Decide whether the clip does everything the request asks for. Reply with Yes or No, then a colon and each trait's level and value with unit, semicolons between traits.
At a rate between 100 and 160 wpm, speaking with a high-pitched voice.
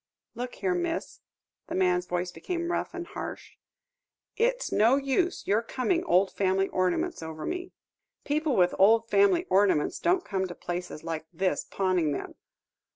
Yes: average, 155 wpm; high, 205 Hz